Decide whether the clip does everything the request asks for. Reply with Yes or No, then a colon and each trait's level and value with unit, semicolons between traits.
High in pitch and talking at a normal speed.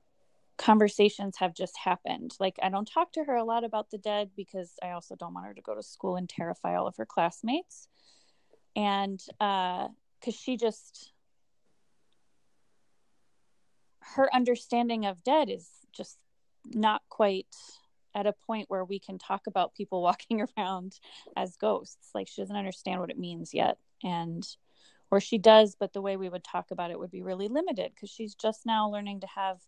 Yes: high, 205 Hz; average, 180 wpm